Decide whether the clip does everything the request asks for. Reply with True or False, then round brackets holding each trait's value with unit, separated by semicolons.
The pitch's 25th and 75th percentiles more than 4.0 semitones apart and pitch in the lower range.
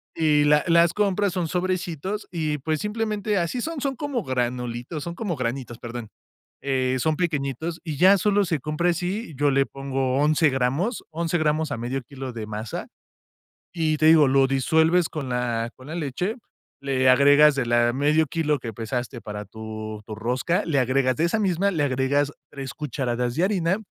False (5.1 semitones; 145 Hz)